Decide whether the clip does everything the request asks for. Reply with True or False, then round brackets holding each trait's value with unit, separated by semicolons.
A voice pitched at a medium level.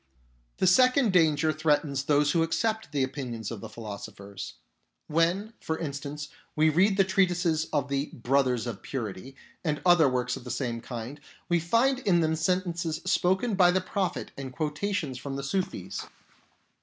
True (155 Hz)